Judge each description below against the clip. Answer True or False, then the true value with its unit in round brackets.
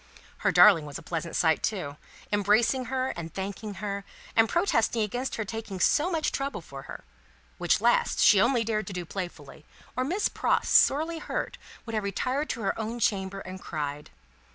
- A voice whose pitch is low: False (210 Hz)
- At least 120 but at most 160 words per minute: False (180 wpm)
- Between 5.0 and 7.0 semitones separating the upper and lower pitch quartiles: True (5.3 semitones)